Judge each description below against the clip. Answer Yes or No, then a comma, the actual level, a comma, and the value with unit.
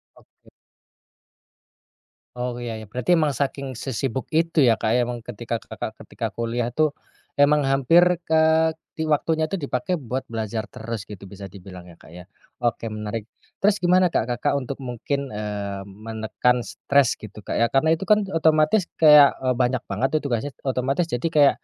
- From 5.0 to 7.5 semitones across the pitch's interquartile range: Yes, wide, 5.4 semitones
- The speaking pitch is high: No, low, 130 Hz